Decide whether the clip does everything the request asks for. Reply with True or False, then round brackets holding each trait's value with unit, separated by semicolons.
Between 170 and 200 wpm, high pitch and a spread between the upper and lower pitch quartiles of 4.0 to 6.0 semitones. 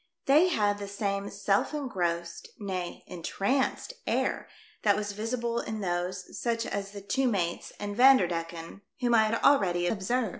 False (155 wpm; 205 Hz; 4.4 semitones)